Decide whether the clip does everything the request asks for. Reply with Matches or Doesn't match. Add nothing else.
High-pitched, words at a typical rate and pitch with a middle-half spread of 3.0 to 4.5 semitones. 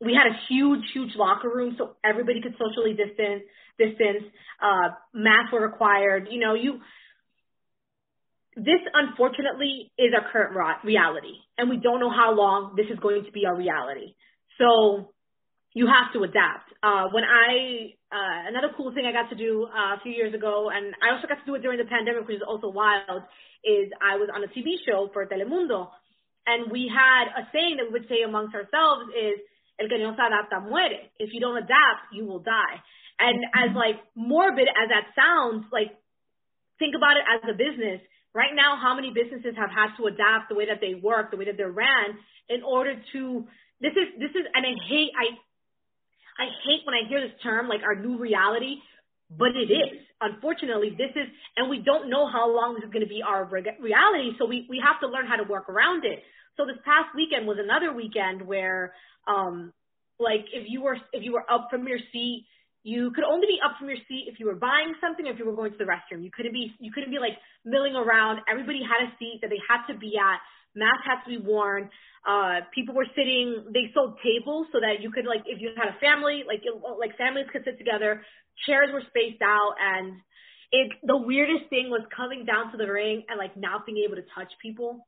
Doesn't match